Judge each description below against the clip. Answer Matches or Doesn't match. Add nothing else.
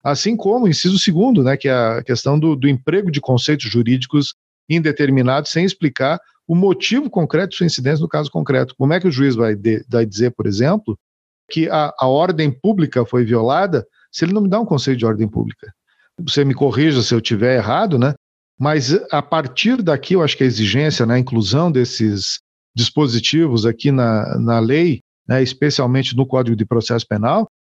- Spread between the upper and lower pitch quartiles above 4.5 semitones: Matches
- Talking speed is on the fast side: Matches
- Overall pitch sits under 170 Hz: Matches